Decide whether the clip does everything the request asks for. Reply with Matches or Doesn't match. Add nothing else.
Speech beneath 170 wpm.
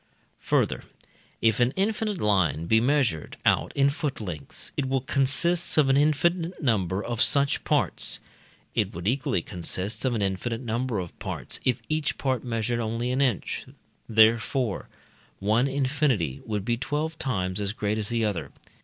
Matches